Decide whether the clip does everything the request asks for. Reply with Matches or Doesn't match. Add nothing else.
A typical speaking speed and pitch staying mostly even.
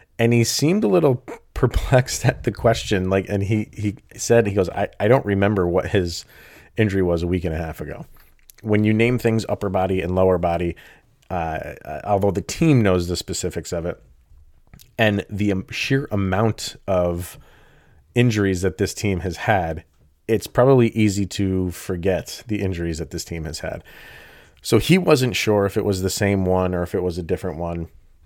Doesn't match